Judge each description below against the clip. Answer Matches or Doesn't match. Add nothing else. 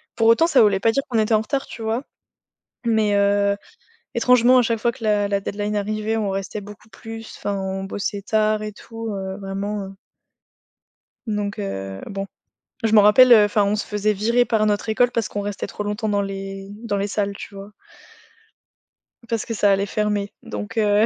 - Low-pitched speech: Doesn't match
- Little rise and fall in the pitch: Matches